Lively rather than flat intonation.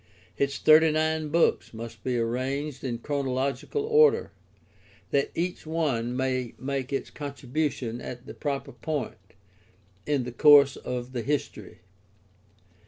No: average, 3.4 semitones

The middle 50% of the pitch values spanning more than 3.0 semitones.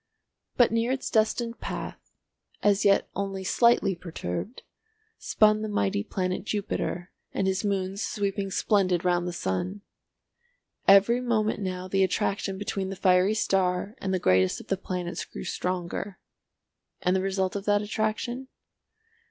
No: narrow, 2.5 semitones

